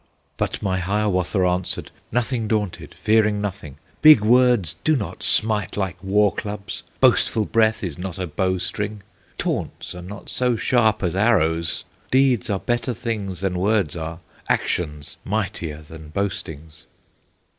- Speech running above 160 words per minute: No, average, 140 wpm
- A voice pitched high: No, low, 100 Hz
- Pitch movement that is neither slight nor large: Yes, average, 3.6 semitones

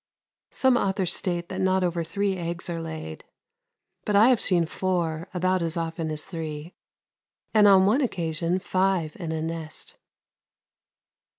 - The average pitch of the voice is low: No, medium, 175 Hz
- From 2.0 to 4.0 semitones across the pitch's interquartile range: Yes, average, 2.7 semitones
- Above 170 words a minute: No, average, 150 wpm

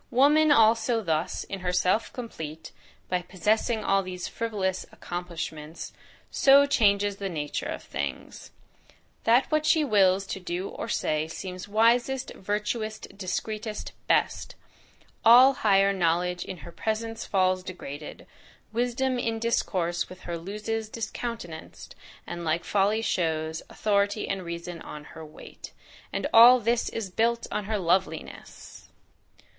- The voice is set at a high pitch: Yes, high, 200 Hz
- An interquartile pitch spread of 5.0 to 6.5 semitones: No, average, 4.4 semitones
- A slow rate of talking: Yes, slow, 130 wpm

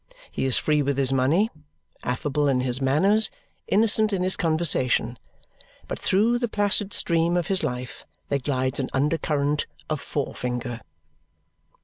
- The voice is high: No, medium, 150 Hz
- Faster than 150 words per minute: No, average, 145 wpm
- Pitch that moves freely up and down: Yes, wide, 6.1 semitones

